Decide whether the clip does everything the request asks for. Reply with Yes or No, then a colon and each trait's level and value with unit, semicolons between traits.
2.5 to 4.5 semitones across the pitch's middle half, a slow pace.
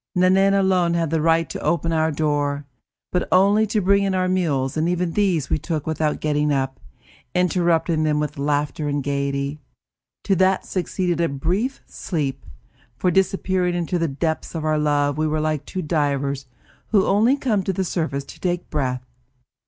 No: average, 4.0 semitones; average, 175 wpm